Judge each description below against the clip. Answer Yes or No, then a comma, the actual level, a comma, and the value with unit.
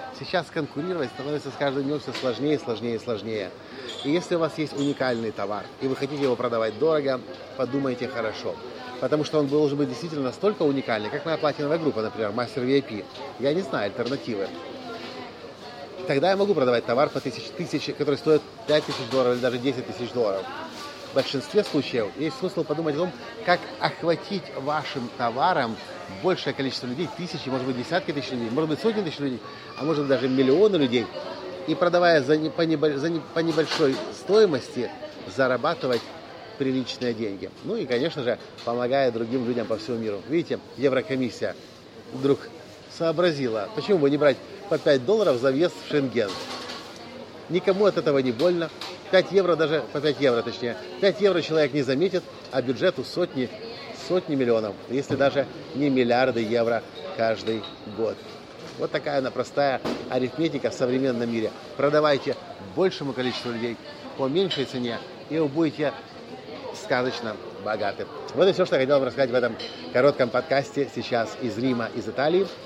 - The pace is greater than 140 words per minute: Yes, fast, 160 wpm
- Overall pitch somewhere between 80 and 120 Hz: No, medium, 140 Hz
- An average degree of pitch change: Yes, average, 4.1 semitones